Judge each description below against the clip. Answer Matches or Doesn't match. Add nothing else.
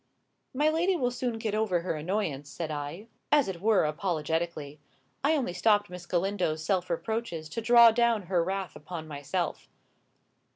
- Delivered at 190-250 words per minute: Doesn't match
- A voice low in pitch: Doesn't match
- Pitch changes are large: Matches